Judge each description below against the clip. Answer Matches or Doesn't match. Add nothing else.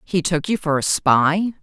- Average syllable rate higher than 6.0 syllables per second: Doesn't match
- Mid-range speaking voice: Matches